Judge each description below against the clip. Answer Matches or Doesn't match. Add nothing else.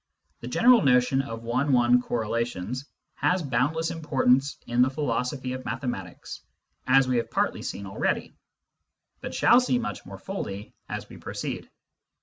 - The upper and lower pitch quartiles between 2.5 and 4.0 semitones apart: Matches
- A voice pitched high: Doesn't match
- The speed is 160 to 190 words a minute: Doesn't match